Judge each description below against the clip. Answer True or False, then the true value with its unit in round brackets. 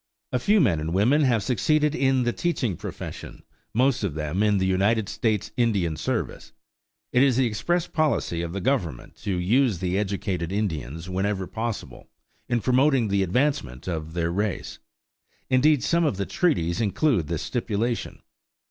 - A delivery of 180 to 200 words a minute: False (165 wpm)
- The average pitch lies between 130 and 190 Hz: False (105 Hz)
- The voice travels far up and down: True (6.2 semitones)